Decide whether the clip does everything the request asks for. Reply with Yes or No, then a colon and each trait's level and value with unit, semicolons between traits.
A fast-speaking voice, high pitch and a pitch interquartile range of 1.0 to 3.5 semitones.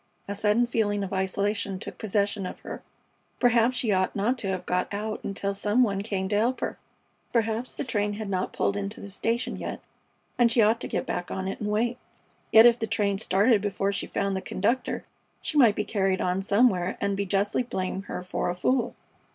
Yes: fast, 210 wpm; high, 205 Hz; average, 2.7 semitones